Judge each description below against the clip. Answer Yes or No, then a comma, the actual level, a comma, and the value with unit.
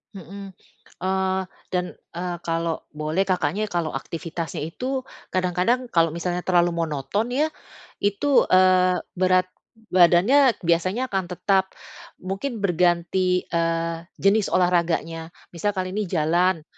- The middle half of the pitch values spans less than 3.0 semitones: Yes, narrow, 2.5 semitones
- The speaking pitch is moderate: Yes, medium, 180 Hz